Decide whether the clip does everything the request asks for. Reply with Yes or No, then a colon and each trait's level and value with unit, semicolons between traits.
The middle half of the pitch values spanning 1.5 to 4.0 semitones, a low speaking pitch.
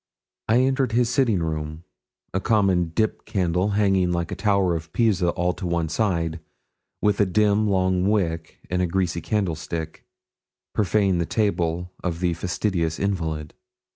Yes: average, 3.6 semitones; very low, 90 Hz